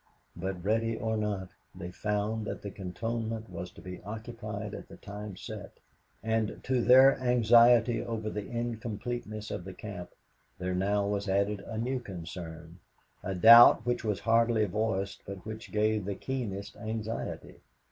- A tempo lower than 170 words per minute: Yes, average, 155 wpm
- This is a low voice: Yes, low, 105 Hz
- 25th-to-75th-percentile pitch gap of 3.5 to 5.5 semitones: No, narrow, 2.6 semitones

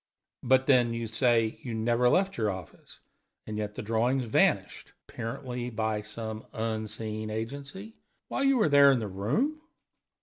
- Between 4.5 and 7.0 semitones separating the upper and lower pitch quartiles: No, average, 3.3 semitones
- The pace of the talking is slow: No, average, 155 wpm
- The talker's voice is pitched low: Yes, low, 115 Hz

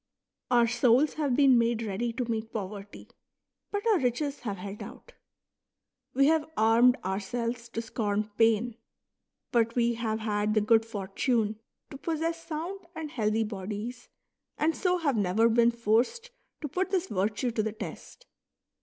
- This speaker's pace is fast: No, average, 155 wpm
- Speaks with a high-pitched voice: Yes, high, 235 Hz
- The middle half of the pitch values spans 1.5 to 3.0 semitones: No, average, 4.5 semitones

